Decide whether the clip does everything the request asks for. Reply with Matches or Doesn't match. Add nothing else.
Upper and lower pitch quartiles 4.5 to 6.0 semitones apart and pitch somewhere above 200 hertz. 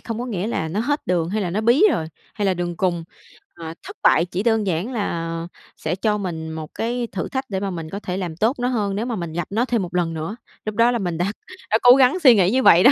Doesn't match